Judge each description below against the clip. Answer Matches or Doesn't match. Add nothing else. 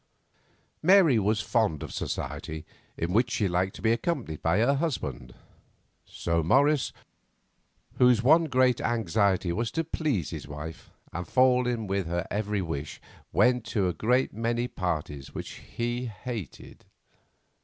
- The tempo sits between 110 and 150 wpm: Matches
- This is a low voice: Matches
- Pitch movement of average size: Doesn't match